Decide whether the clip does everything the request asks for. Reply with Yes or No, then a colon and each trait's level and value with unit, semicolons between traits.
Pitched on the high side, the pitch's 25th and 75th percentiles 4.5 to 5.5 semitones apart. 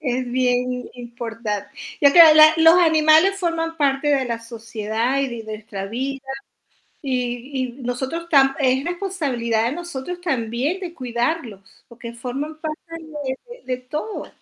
Yes: very high, 265 Hz; average, 4.8 semitones